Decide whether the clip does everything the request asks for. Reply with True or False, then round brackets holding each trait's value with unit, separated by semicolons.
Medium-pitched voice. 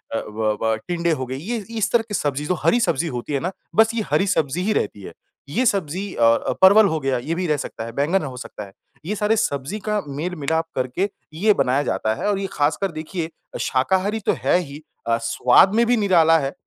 True (165 Hz)